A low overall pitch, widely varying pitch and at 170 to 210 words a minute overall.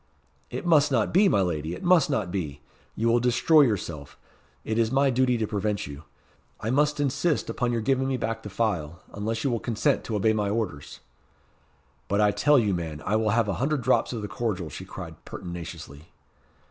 Yes: low, 110 Hz; wide, 6.1 semitones; average, 200 wpm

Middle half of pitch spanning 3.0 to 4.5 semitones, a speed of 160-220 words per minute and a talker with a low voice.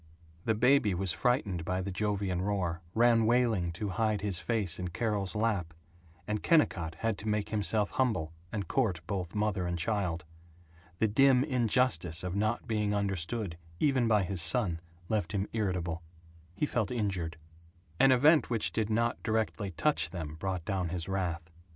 Yes: average, 4.1 semitones; average, 165 wpm; low, 100 Hz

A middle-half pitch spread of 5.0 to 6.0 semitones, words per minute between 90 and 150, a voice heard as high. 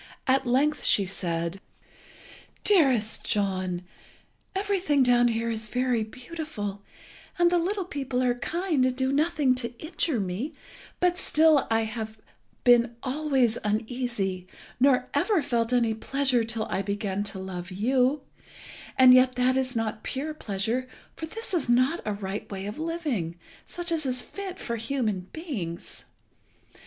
Yes: wide, 5.5 semitones; average, 145 wpm; very high, 250 Hz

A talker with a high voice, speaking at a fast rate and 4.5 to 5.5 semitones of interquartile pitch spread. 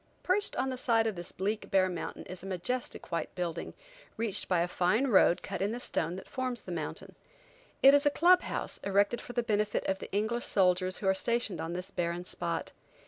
Yes: high, 195 Hz; fast, 215 wpm; average, 4.9 semitones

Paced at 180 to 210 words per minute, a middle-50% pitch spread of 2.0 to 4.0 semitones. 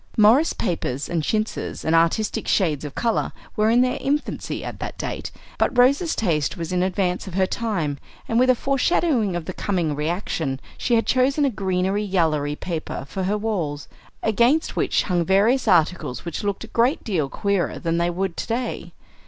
No: average, 185 wpm; wide, 5.5 semitones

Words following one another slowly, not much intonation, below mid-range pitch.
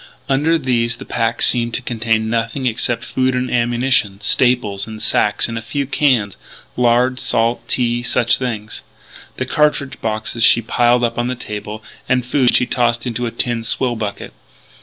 No: average, 170 wpm; narrow, 1.8 semitones; low, 120 Hz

